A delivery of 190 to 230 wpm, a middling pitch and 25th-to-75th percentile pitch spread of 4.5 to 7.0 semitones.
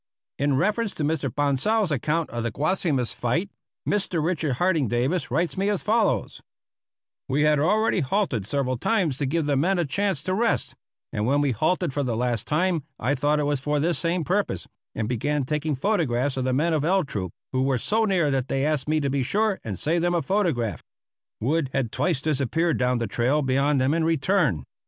Yes: fast, 205 wpm; medium, 150 Hz; average, 5.1 semitones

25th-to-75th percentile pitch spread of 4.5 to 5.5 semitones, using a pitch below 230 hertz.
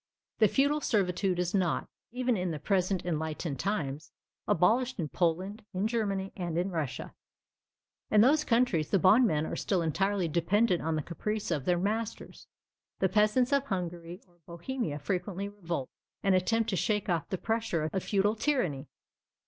No: average, 4.1 semitones; high, 190 Hz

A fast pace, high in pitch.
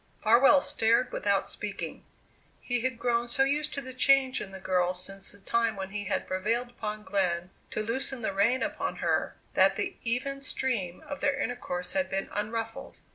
No: average, 185 wpm; high, 225 Hz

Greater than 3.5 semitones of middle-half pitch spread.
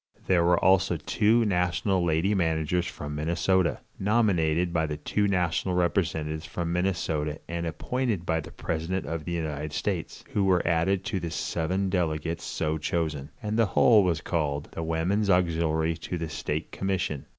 No: average, 2.9 semitones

